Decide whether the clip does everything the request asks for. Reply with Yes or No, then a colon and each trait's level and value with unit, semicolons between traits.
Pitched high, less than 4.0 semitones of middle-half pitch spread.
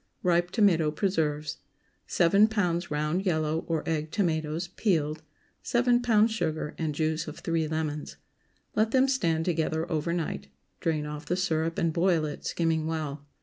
No: medium, 165 Hz; average, 2.8 semitones